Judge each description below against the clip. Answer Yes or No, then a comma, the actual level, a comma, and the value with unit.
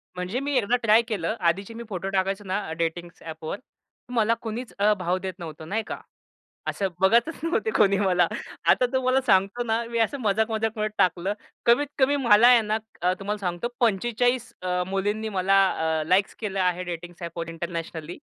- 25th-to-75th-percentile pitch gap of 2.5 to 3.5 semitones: No, average, 4.0 semitones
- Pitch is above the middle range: Yes, high, 200 Hz